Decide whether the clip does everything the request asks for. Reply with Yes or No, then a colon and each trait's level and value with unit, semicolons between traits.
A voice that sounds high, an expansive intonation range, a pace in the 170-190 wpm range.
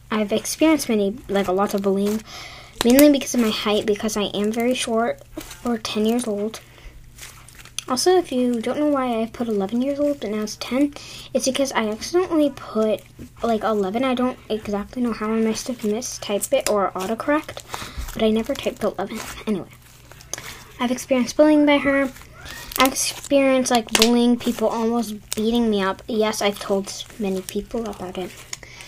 No: high, 225 Hz; average, 3.7 semitones; average, 175 wpm